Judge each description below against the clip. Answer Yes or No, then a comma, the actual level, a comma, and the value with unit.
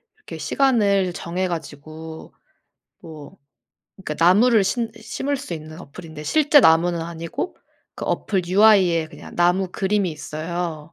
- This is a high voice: No, medium, 175 Hz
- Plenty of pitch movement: No, average, 4.2 semitones